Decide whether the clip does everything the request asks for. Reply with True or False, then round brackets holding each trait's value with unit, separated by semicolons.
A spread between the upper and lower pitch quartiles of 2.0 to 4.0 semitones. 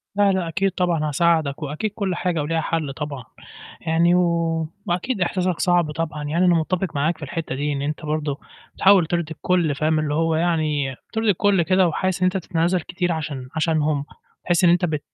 True (2.9 semitones)